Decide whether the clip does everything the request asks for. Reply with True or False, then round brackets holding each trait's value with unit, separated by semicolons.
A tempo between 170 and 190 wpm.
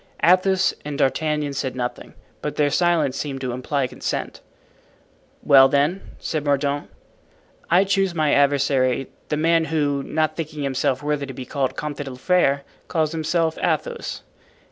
False (155 wpm)